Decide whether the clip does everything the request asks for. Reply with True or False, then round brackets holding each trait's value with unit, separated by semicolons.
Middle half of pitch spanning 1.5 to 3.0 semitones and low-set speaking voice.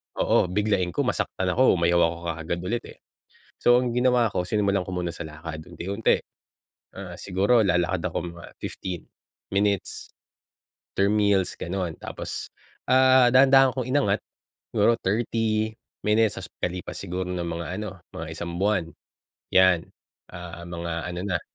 False (3.9 semitones; 95 Hz)